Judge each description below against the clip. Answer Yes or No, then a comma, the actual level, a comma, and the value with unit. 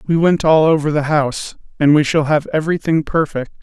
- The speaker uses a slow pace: No, average, 200 wpm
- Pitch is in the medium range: Yes, medium, 150 Hz